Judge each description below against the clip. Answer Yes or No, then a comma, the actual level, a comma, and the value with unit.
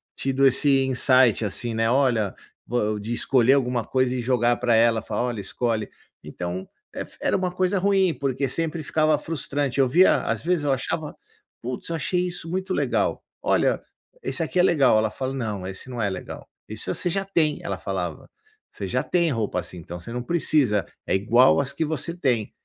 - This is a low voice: Yes, low, 130 Hz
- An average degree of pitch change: No, wide, 5.7 semitones